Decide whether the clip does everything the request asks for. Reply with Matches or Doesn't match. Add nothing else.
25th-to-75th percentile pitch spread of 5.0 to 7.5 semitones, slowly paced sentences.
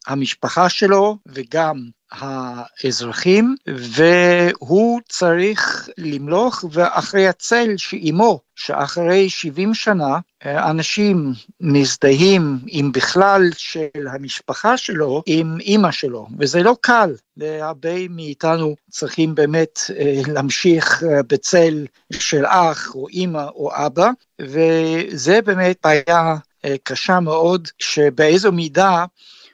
Doesn't match